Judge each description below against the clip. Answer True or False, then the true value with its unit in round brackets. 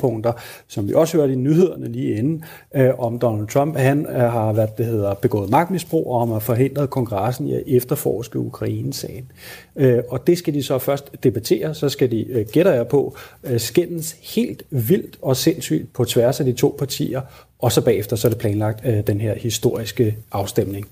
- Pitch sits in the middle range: False (125 Hz)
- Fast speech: False (180 wpm)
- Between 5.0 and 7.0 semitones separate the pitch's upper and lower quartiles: False (3.8 semitones)